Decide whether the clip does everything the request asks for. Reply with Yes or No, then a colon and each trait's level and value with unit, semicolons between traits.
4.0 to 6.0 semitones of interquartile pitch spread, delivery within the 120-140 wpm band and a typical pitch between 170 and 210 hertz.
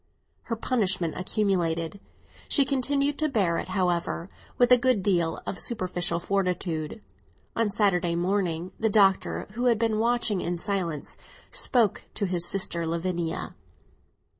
Yes: average, 4.5 semitones; slow, 135 wpm; high, 190 Hz